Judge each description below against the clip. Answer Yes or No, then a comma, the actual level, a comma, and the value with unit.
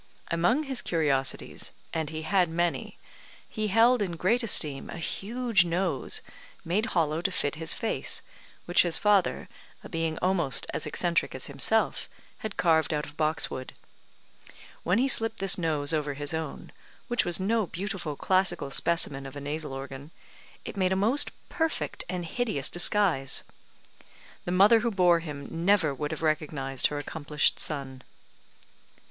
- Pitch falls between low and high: Yes, medium, 170 Hz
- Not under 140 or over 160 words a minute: Yes, average, 155 wpm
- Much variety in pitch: No, average, 4.7 semitones